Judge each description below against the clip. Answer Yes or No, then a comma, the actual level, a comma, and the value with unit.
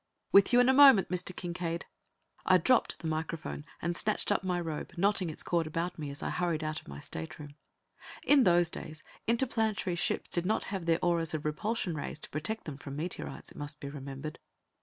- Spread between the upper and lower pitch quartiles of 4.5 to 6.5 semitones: No, average, 3.9 semitones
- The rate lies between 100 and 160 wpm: No, average, 200 wpm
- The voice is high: No, medium, 170 Hz